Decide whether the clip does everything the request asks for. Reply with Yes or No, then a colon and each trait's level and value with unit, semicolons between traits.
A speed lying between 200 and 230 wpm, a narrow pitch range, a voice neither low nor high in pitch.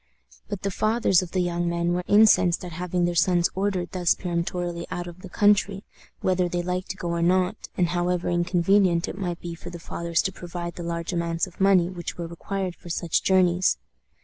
Yes: fast, 205 wpm; narrow, 1.4 semitones; medium, 175 Hz